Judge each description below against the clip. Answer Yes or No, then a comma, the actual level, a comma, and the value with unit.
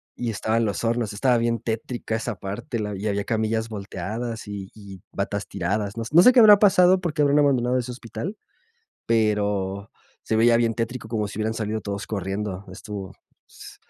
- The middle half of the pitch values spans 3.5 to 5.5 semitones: No, average, 2.8 semitones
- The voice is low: Yes, low, 110 Hz